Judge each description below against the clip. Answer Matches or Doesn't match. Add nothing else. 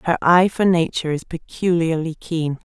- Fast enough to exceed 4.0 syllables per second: Matches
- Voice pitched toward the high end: Doesn't match